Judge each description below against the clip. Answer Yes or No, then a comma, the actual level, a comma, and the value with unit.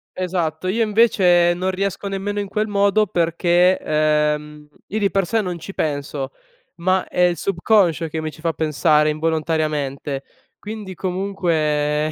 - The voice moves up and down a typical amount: Yes, average, 4.1 semitones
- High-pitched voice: No, medium, 175 Hz